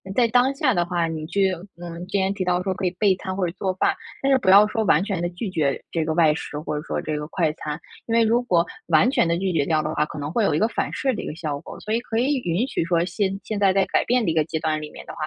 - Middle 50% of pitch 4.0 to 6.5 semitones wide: Yes, average, 4.9 semitones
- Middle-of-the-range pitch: Yes, medium, 180 Hz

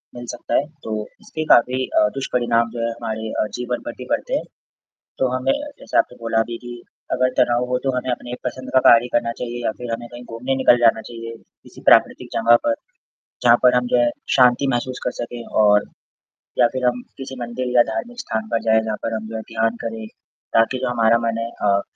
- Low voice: Yes, low, 120 Hz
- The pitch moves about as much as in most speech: No, narrow, 1.6 semitones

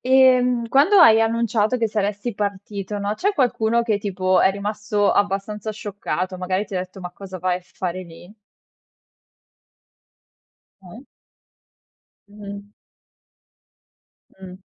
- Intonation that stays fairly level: No, average, 3.0 semitones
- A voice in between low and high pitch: No, high, 205 Hz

